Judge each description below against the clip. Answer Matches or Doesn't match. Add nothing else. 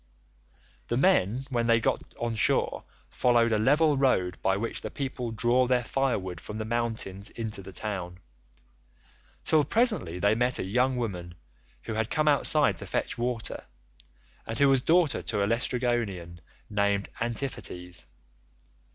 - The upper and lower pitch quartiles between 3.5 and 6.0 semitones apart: Matches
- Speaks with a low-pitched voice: Matches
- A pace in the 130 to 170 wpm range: Matches